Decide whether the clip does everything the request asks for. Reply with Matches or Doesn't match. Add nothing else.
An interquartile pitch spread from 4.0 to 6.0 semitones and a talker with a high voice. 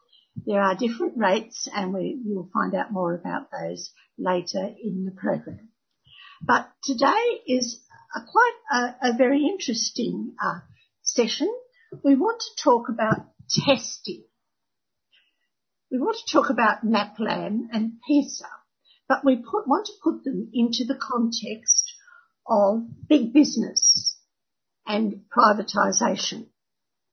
Matches